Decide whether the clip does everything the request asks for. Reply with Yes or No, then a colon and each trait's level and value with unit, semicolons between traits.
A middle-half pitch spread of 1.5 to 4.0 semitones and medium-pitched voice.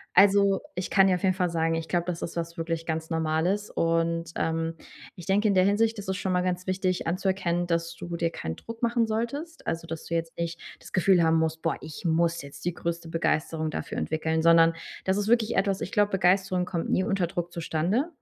Yes: average, 2.7 semitones; medium, 175 Hz